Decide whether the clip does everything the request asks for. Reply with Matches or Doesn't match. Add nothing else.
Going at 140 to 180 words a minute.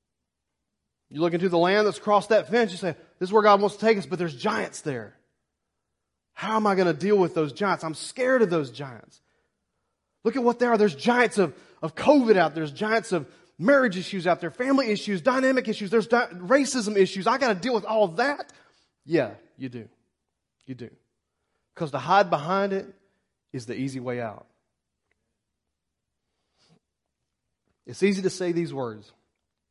Doesn't match